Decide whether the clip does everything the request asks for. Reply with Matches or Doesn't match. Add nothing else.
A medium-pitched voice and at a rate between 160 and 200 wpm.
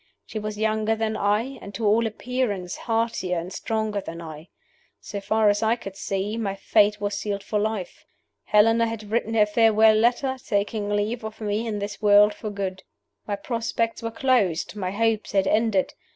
Doesn't match